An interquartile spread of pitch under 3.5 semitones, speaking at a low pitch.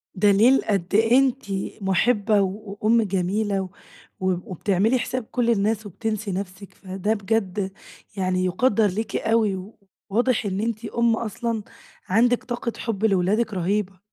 No: average, 2.9 semitones; high, 210 Hz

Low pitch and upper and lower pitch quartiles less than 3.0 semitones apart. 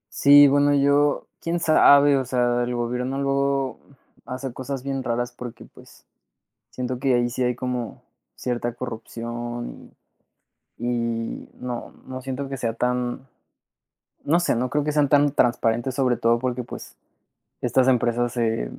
Yes: low, 125 Hz; narrow, 2.4 semitones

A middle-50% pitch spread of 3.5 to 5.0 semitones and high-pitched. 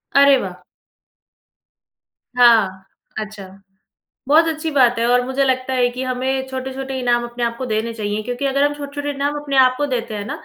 No: average, 3.0 semitones; very high, 255 Hz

